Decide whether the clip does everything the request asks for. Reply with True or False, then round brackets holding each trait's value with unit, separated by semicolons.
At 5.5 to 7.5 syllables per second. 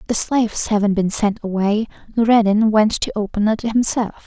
False (5.3 syllables/s)